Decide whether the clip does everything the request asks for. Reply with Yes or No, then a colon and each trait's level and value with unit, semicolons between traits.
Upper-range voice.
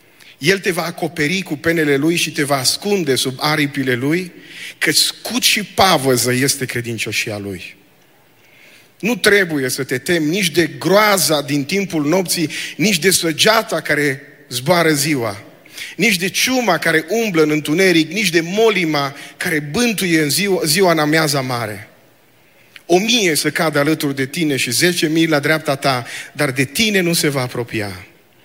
No: medium, 155 Hz